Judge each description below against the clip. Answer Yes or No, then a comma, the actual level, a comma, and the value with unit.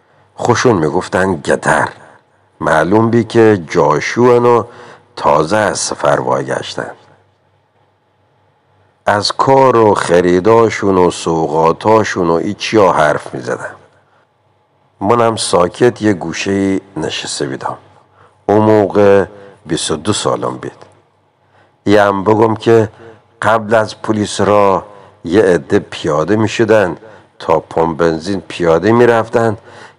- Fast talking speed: No, slow, 105 wpm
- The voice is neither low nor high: No, low, 105 Hz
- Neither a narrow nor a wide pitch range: Yes, average, 3.1 semitones